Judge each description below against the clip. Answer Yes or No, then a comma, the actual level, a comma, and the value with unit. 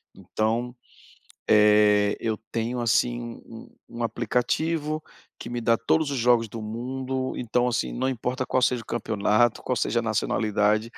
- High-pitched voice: No, low, 120 Hz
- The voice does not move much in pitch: Yes, narrow, 2.3 semitones